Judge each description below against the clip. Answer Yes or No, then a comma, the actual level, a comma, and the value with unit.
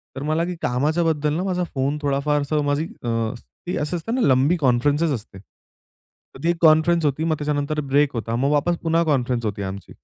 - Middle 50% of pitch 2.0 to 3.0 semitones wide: No, average, 3.5 semitones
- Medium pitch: Yes, medium, 150 Hz